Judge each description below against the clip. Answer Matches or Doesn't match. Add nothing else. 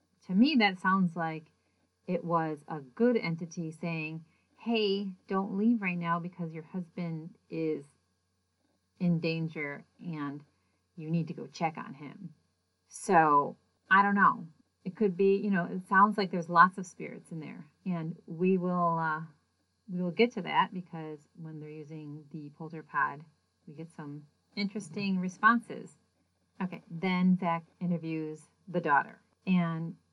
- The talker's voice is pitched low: Doesn't match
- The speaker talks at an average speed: Matches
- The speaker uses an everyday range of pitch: Matches